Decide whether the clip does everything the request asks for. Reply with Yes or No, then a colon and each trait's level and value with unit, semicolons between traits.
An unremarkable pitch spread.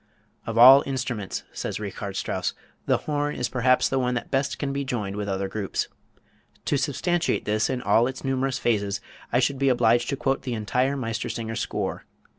Yes: average, 3.1 semitones